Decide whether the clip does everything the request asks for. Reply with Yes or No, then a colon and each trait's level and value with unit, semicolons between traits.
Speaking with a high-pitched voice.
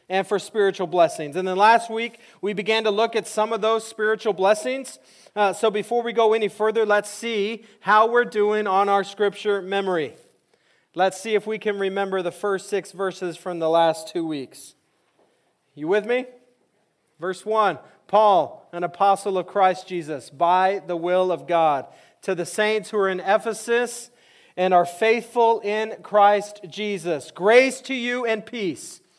Yes: high, 205 Hz